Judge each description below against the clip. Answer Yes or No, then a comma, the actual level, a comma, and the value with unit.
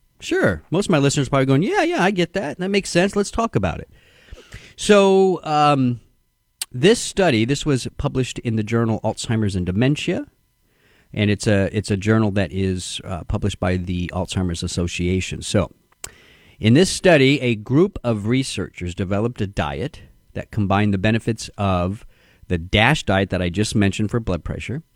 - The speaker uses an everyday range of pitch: No, wide, 7.1 semitones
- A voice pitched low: Yes, low, 110 Hz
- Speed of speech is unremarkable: Yes, average, 175 wpm